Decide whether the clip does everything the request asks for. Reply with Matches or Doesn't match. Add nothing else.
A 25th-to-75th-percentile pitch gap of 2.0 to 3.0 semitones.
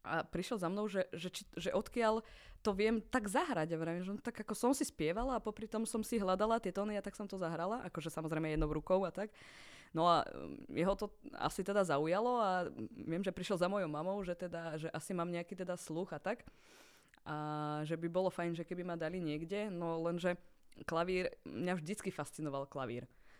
Doesn't match